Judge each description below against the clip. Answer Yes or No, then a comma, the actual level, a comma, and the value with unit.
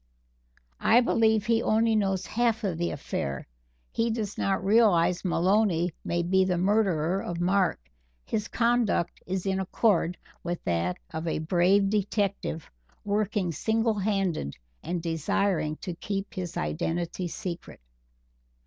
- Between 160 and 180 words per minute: No, slow, 135 wpm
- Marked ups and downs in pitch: No, average, 3.6 semitones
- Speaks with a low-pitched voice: No, high, 190 Hz